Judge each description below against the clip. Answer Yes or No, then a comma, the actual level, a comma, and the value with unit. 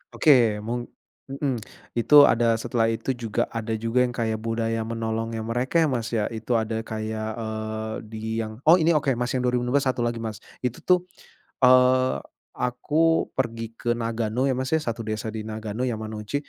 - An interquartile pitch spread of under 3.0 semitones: Yes, narrow, 2.4 semitones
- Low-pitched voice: Yes, low, 115 Hz